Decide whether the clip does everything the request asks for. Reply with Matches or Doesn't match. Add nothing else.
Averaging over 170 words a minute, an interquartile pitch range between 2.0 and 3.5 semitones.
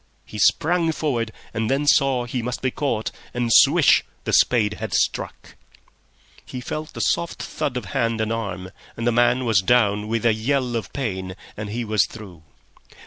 Matches